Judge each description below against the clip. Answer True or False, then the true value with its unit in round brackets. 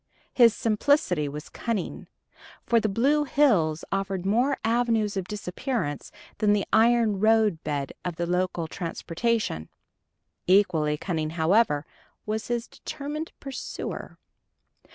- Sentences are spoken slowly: True (110 wpm)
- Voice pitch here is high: True (205 Hz)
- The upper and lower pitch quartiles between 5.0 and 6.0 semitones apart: True (5.6 semitones)